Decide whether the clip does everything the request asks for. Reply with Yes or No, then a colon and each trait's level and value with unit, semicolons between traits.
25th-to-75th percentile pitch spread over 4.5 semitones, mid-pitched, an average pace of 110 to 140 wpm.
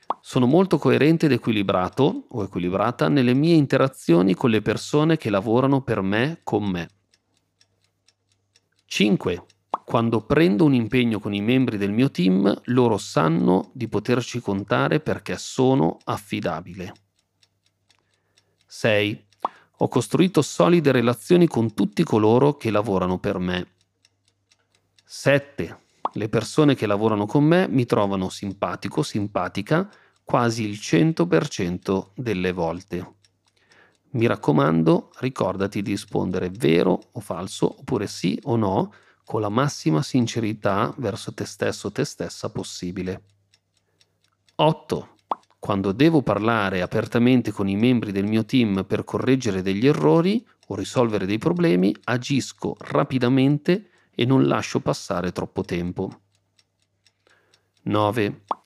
No: average, 5.2 semitones; low, 105 Hz; average, 120 wpm